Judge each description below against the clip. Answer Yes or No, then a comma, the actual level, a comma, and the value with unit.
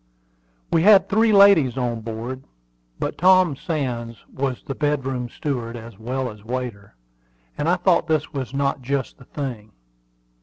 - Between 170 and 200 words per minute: No, average, 150 wpm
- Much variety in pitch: No, average, 4.2 semitones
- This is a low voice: Yes, low, 130 Hz